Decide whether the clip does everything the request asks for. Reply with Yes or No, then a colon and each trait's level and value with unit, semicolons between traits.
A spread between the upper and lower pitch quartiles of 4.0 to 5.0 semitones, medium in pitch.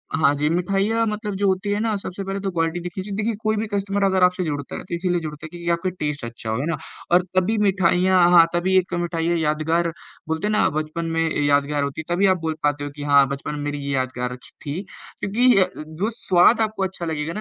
Yes: average, 4.4 semitones; medium, 175 Hz